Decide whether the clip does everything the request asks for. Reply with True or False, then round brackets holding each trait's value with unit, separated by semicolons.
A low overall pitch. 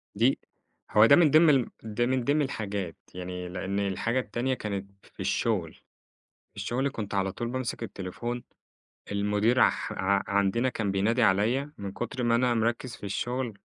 True (115 Hz)